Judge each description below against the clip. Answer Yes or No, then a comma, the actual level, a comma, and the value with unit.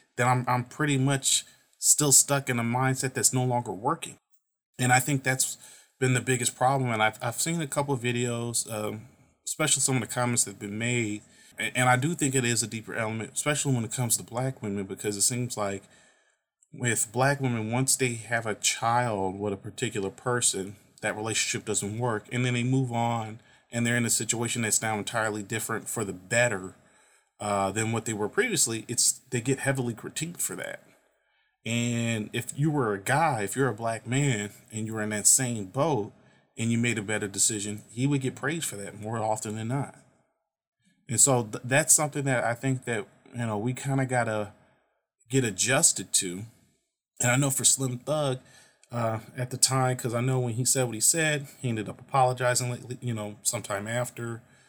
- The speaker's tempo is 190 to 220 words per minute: Yes, fast, 205 wpm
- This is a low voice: Yes, low, 120 Hz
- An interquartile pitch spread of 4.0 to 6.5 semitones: No, average, 3.1 semitones